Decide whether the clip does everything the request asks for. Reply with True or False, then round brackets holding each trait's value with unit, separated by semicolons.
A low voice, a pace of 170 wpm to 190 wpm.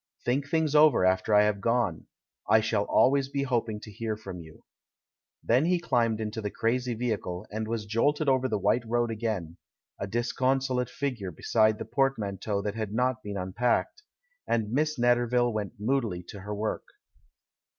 True (115 Hz; 180 wpm)